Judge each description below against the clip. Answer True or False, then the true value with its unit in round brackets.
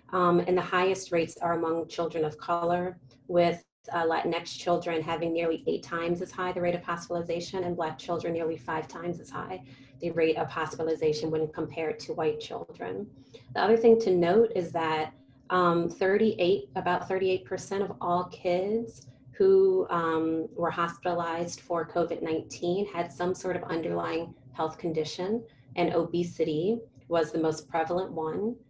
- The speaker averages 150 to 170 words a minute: True (155 wpm)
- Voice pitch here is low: False (170 Hz)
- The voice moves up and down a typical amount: False (2.1 semitones)